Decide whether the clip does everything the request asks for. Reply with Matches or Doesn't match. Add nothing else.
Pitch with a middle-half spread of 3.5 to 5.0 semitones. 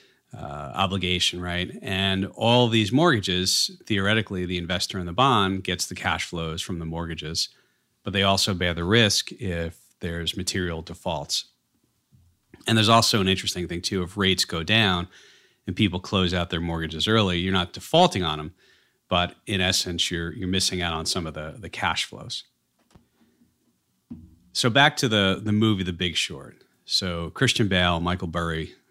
Doesn't match